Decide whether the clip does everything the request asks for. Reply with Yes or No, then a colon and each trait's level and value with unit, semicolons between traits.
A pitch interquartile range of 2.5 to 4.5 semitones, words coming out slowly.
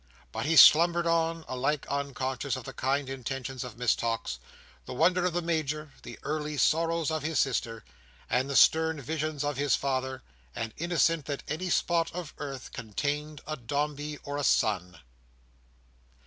No: average, 3.5 semitones; average, 160 wpm